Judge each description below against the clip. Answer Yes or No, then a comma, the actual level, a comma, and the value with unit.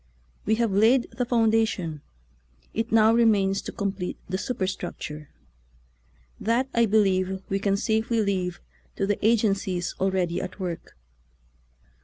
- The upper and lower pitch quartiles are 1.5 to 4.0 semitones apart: Yes, average, 3.1 semitones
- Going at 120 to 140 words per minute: Yes, slow, 135 wpm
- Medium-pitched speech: No, high, 200 Hz